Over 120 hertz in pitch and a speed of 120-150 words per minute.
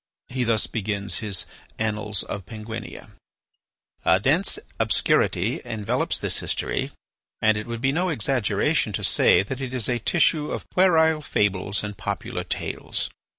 No: low, 110 Hz; average, 145 wpm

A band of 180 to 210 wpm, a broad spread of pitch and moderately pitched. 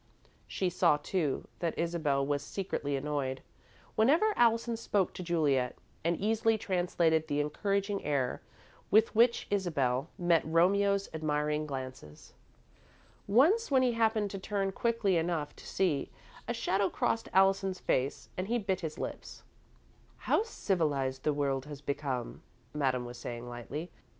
No: average, 140 wpm; wide, 5.8 semitones; medium, 170 Hz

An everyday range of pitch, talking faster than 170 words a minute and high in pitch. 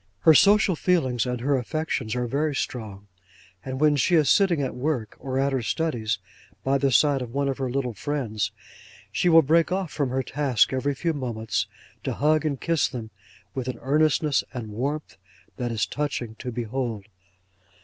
No: average, 3.8 semitones; average, 180 wpm; low, 135 Hz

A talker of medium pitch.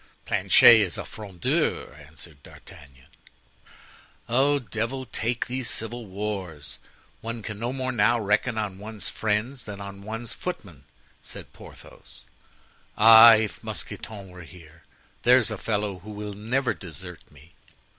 No: low, 105 Hz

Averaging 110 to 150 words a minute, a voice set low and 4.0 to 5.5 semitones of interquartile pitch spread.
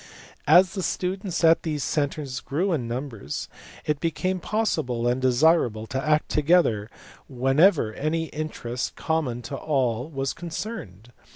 No: slow, 135 wpm; medium, 145 Hz; average, 5.2 semitones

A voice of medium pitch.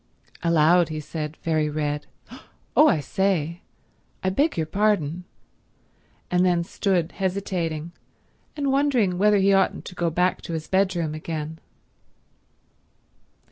Yes: medium, 175 Hz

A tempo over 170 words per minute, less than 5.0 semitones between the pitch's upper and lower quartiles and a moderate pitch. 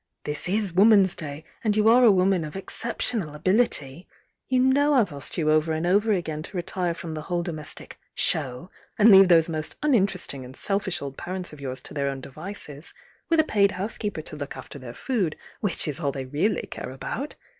No: fast, 205 wpm; wide, 5.5 semitones; medium, 175 Hz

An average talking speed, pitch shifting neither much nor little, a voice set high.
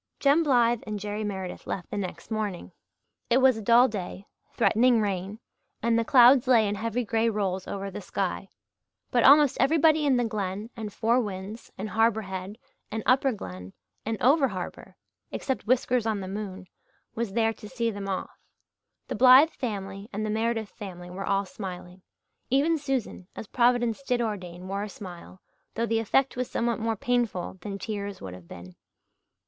Yes: average, 175 wpm; average, 3.7 semitones; high, 215 Hz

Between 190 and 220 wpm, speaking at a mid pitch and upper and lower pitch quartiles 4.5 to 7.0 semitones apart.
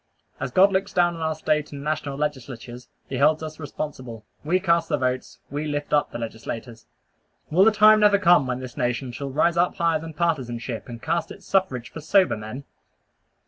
Yes: average, 195 wpm; medium, 150 Hz; average, 5.0 semitones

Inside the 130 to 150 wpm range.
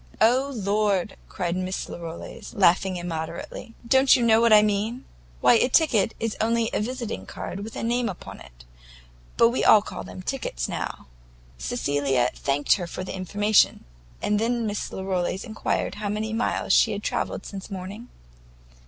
No: average, 165 wpm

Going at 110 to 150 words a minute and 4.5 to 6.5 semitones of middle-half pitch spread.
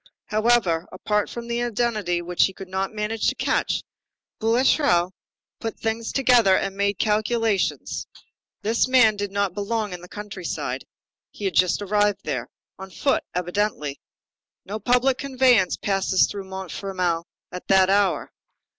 No: average, 145 wpm; average, 3.2 semitones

